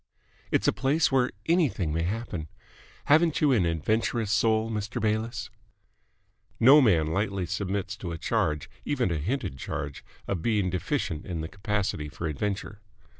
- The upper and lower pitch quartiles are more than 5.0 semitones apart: Yes, wide, 5.4 semitones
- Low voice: Yes, low, 100 Hz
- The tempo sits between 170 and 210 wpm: No, average, 150 wpm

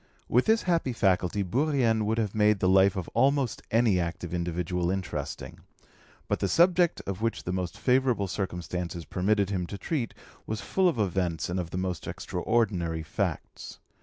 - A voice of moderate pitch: No, low, 100 Hz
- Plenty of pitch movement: No, average, 4.8 semitones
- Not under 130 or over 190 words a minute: Yes, average, 165 wpm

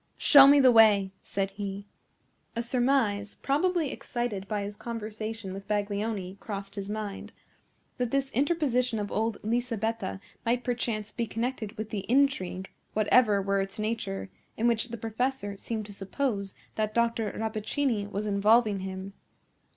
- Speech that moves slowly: No, average, 145 wpm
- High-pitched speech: Yes, high, 215 Hz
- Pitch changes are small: No, average, 3.1 semitones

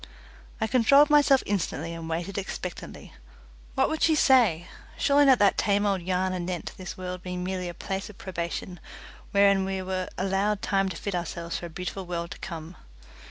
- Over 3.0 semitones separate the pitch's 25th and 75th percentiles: No, narrow, 2.5 semitones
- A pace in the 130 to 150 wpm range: No, average, 180 wpm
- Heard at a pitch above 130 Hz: Yes, high, 190 Hz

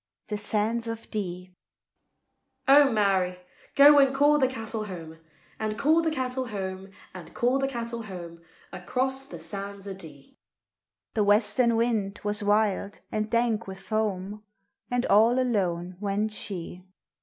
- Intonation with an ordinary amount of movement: Yes, average, 4.0 semitones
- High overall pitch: Yes, high, 215 Hz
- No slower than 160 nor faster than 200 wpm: No, average, 145 wpm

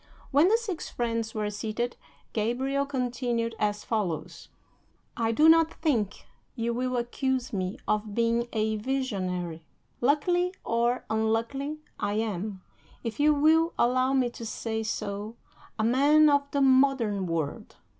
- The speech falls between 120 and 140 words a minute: Yes, slow, 135 wpm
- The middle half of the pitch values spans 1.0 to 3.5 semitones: No, average, 4.2 semitones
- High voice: Yes, high, 235 Hz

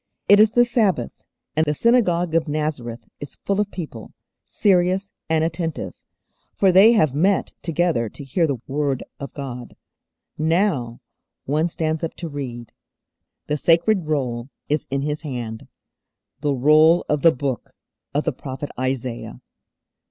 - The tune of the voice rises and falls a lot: No, average, 4.5 semitones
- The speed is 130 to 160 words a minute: Yes, average, 145 wpm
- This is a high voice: No, medium, 155 Hz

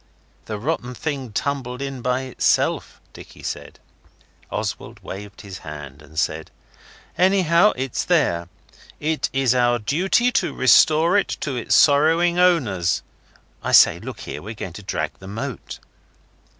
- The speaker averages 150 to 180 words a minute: No, slow, 135 wpm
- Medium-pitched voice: No, low, 130 Hz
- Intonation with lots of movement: Yes, wide, 7.5 semitones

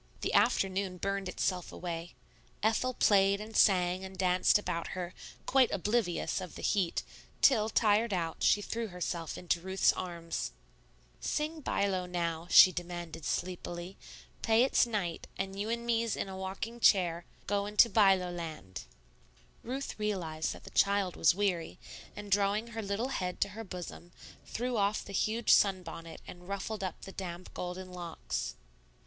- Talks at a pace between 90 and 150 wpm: No, average, 160 wpm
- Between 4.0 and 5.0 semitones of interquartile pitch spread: No, average, 3.0 semitones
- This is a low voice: No, high, 190 Hz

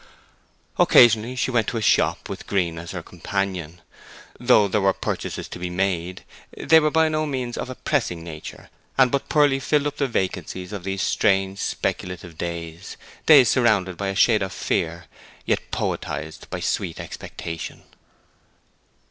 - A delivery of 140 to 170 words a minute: Yes, average, 160 wpm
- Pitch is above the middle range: No, low, 100 Hz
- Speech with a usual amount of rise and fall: No, wide, 6.2 semitones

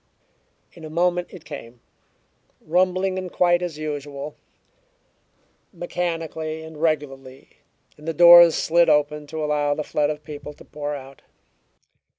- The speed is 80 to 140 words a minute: Yes, slow, 135 wpm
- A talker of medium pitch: Yes, medium, 155 Hz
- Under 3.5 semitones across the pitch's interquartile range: Yes, average, 2.8 semitones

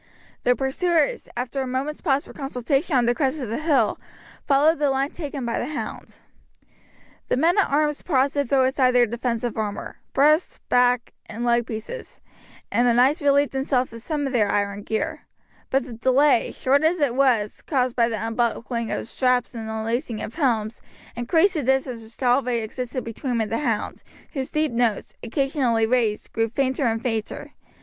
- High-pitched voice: Yes, very high, 250 Hz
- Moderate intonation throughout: Yes, average, 3.3 semitones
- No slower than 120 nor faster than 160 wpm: No, average, 185 wpm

